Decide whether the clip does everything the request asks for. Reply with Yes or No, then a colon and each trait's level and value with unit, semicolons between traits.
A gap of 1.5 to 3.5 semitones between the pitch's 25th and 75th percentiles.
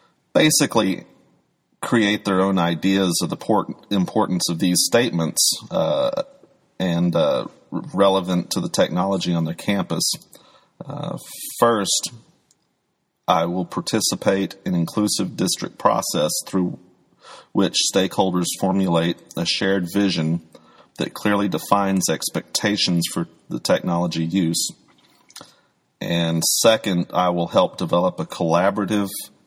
Yes: average, 3.1 semitones